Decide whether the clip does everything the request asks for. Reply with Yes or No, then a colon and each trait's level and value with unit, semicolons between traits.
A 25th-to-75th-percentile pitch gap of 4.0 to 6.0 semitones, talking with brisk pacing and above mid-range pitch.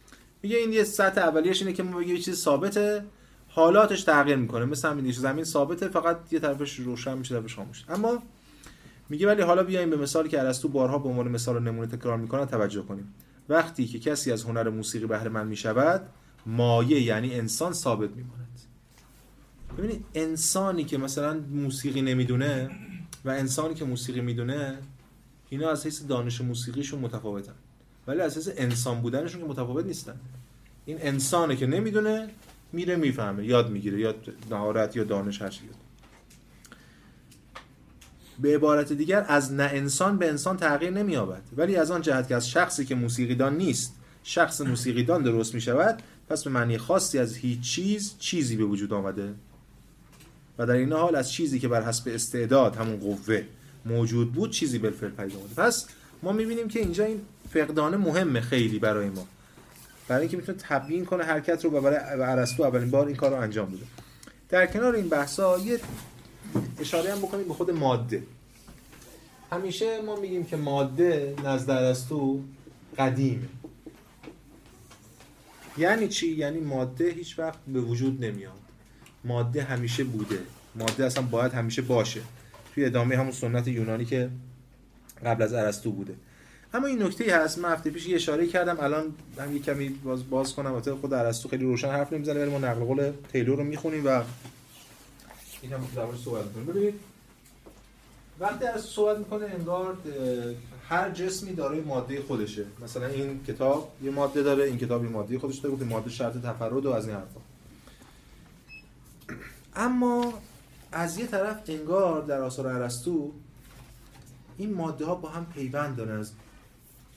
No: average, 5.3 semitones; fast, 160 wpm; low, 135 Hz